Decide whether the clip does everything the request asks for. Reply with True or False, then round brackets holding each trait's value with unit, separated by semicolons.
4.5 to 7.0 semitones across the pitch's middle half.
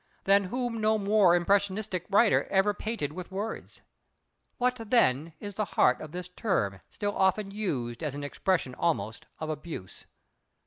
True (5.1 semitones)